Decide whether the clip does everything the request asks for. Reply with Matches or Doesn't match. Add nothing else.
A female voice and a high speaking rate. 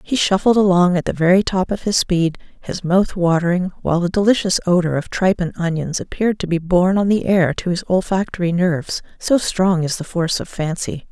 Matches